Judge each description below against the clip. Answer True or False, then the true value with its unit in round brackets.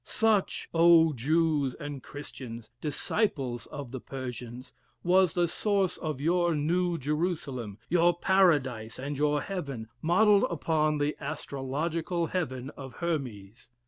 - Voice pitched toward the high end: False (150 Hz)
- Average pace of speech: False (120 wpm)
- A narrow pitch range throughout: False (4.6 semitones)